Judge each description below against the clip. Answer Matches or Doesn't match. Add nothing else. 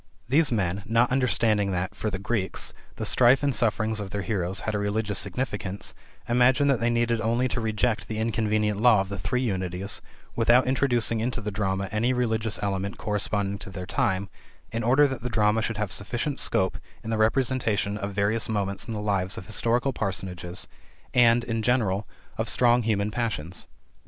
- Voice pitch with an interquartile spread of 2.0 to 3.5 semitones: Matches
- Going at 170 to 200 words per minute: Matches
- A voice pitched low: Matches